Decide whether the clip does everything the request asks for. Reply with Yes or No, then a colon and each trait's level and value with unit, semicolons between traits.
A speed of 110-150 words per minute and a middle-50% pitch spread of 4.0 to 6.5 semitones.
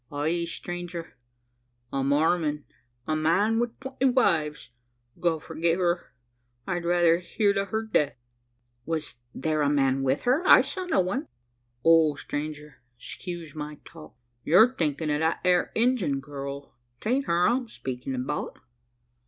Yes: average, 140 wpm; average, 4.3 semitones